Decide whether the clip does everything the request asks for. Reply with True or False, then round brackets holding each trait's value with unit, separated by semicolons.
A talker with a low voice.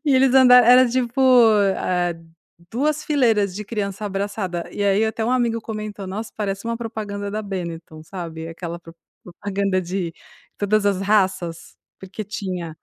False (200 Hz)